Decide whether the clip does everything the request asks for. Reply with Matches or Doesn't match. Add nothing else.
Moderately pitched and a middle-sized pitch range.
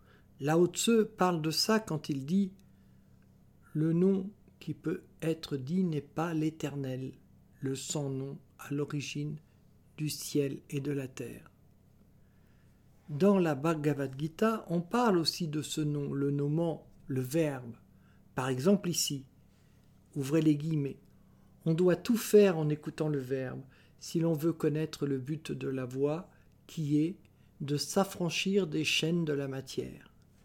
Matches